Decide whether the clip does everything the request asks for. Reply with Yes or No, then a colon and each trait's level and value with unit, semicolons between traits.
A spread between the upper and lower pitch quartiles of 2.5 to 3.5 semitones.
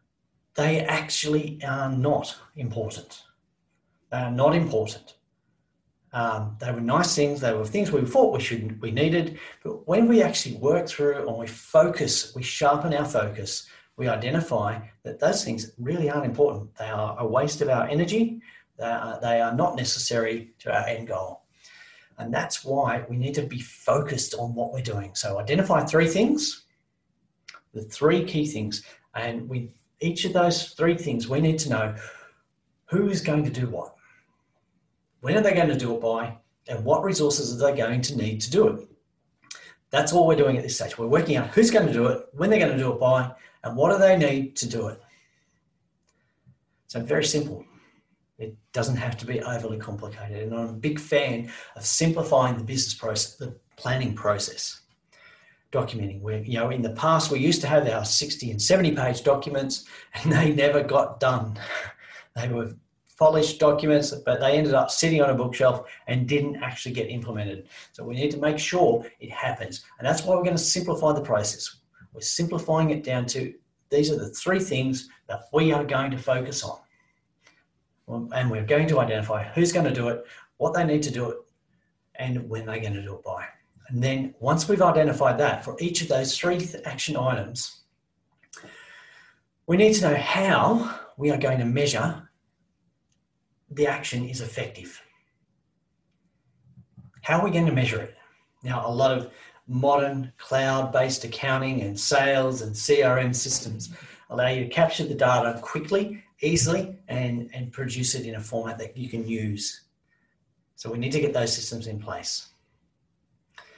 No: average, 4.7 semitones